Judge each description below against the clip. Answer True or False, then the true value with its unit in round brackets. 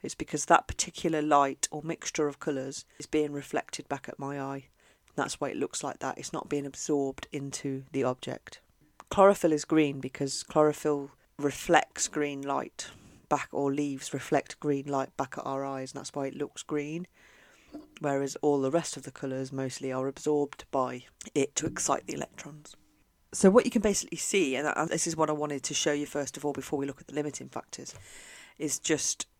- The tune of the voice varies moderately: False (1.9 semitones)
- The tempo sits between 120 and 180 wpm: False (200 wpm)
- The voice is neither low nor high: True (145 Hz)